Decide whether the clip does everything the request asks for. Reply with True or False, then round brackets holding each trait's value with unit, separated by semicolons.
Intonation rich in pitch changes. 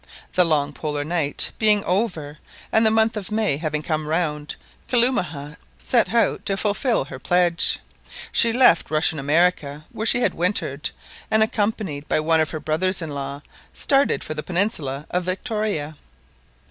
True (6.0 semitones)